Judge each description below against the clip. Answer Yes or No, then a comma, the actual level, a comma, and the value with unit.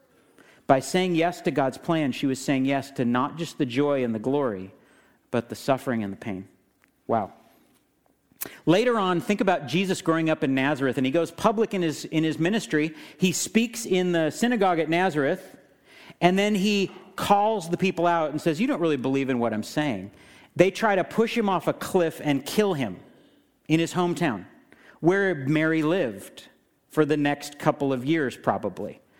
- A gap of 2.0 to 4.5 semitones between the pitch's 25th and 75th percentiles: No, average, 4.9 semitones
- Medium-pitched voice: Yes, medium, 160 Hz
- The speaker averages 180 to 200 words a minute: Yes, average, 185 wpm